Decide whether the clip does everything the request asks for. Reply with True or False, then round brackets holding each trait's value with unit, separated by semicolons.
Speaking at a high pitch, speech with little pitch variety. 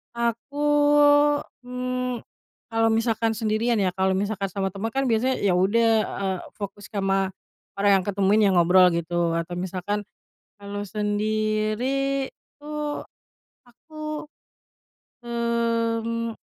False (215 Hz; 3.3 semitones)